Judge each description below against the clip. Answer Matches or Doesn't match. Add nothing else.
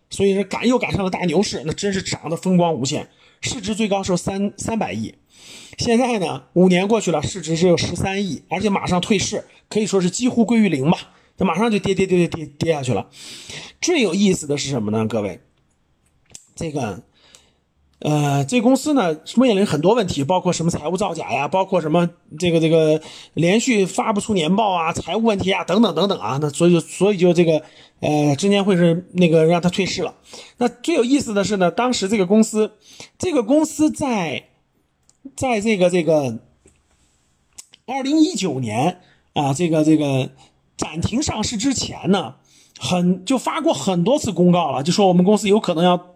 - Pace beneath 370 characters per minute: Matches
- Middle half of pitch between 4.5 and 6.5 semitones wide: Matches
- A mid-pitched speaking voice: Matches